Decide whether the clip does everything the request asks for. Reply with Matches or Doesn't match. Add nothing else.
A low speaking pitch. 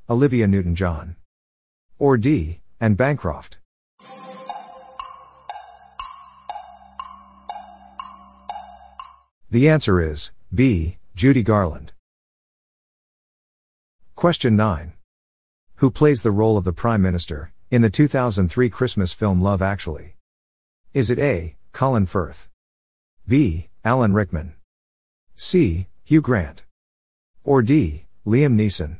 Matches